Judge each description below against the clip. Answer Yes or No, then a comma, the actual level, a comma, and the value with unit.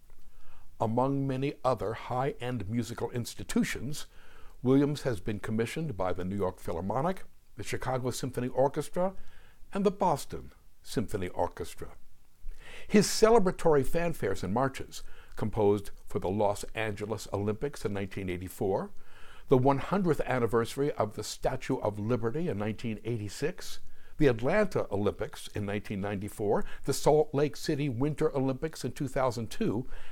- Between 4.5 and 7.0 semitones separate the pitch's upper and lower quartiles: Yes, average, 5.3 semitones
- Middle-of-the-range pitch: No, low, 125 Hz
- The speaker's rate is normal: No, slow, 120 wpm